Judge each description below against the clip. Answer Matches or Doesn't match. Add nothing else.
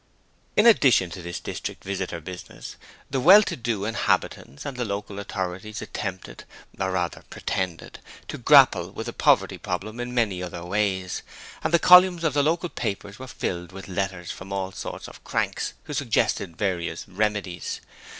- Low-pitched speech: Matches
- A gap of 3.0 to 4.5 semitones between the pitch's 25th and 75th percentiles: Doesn't match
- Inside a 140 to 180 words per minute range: Matches